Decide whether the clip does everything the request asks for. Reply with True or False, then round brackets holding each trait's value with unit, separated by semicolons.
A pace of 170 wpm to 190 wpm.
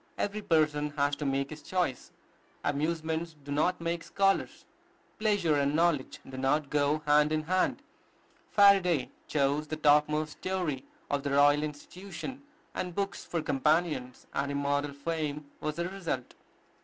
False (145 wpm)